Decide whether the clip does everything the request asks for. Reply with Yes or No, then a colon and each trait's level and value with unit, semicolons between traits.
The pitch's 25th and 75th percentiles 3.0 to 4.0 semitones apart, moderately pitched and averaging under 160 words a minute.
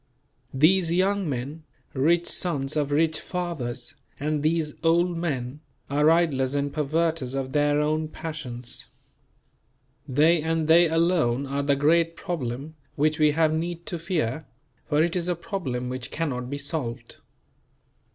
Yes: average, 3.4 semitones; medium, 155 Hz; average, 140 wpm